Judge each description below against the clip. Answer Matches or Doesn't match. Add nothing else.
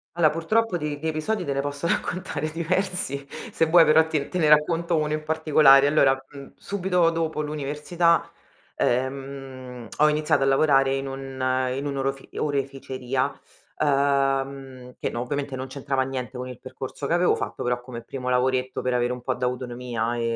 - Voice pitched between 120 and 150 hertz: Matches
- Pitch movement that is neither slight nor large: Matches